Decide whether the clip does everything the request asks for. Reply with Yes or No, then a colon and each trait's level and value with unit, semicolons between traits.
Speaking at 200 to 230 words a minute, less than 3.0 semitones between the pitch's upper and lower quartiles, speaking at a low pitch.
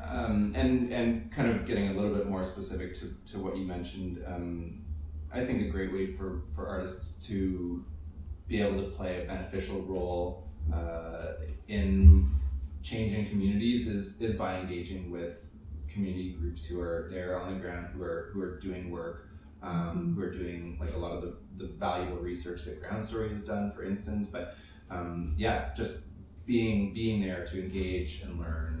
No: average, 180 wpm; narrow, 2.6 semitones; very low, 90 Hz